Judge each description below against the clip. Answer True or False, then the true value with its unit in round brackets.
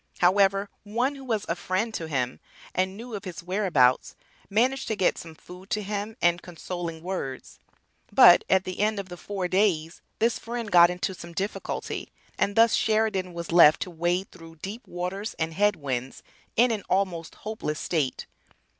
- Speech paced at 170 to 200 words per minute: True (175 wpm)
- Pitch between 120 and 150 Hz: False (185 Hz)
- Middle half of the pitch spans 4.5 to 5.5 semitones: False (3.7 semitones)